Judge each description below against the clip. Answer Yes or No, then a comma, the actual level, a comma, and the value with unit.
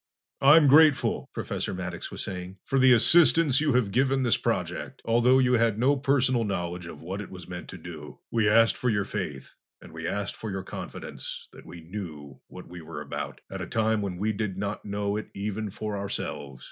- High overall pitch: No, low, 105 Hz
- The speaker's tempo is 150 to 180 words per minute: No, fast, 205 wpm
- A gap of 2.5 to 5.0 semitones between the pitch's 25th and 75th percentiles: No, wide, 5.5 semitones